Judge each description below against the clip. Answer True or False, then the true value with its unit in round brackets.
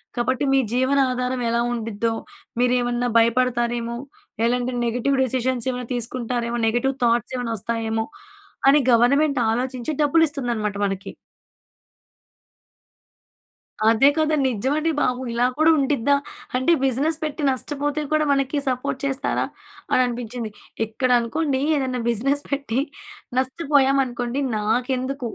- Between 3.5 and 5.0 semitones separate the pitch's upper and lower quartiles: False (2.6 semitones)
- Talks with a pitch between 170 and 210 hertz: False (250 Hz)